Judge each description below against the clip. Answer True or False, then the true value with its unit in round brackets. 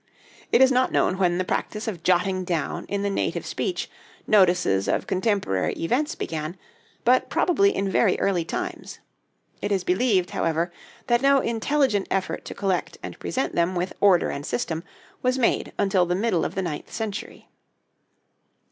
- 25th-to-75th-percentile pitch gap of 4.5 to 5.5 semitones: True (4.8 semitones)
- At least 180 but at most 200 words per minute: False (165 wpm)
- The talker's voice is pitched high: True (195 Hz)